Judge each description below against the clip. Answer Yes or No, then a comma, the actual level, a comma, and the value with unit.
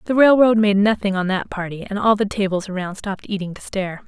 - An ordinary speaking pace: No, fast, 235 wpm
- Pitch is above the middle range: Yes, high, 200 Hz